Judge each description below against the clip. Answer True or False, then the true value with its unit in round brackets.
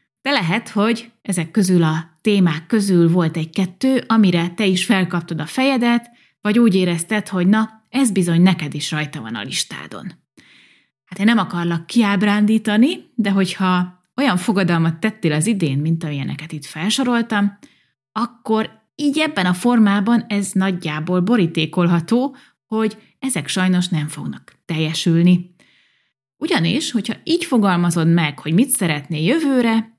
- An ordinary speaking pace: True (135 wpm)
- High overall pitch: True (195 Hz)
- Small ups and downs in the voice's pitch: False (5.1 semitones)